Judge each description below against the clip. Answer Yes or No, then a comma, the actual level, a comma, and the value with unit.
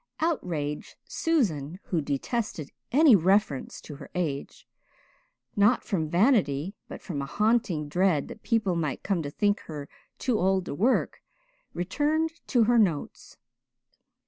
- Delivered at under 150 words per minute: Yes, slow, 135 wpm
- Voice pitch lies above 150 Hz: Yes, medium, 185 Hz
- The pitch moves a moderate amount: No, wide, 7.0 semitones